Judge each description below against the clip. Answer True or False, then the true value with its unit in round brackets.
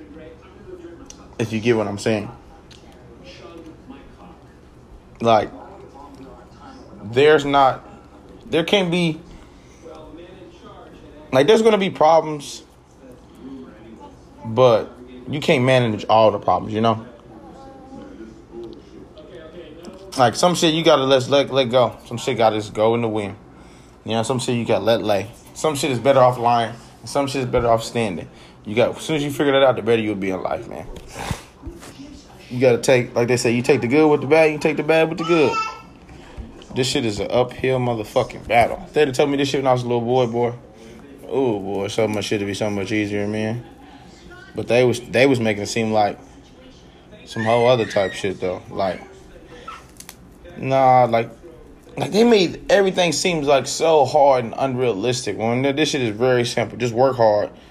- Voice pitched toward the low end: True (125 Hz)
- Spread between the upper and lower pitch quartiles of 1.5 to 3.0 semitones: False (4.7 semitones)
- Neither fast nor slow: True (175 wpm)